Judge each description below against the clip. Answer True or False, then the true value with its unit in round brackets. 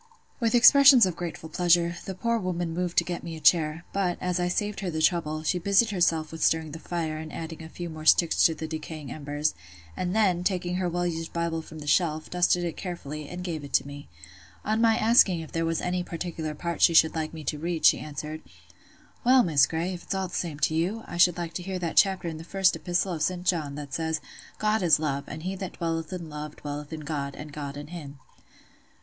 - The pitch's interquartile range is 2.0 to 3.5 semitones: True (2.5 semitones)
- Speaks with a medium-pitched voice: True (170 Hz)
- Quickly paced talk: True (235 wpm)